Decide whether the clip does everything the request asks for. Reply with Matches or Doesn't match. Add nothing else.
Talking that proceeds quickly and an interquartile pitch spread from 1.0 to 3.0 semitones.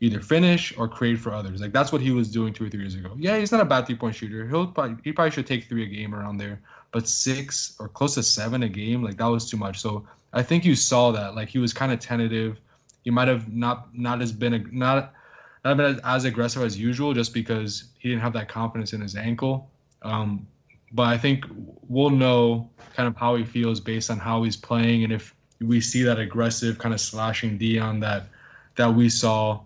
Matches